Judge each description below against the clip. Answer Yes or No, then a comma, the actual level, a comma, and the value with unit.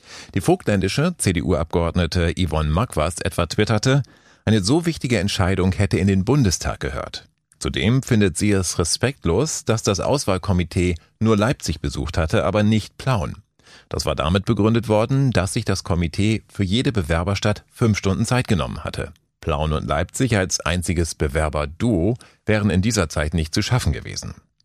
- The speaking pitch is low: Yes, low, 100 Hz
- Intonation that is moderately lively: Yes, average, 4.6 semitones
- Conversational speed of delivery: Yes, average, 150 wpm